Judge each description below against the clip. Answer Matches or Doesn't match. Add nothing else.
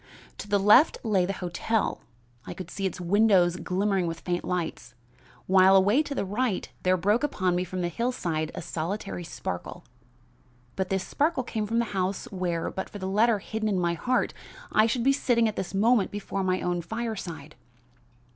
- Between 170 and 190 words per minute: Matches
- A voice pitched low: Doesn't match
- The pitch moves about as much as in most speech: Matches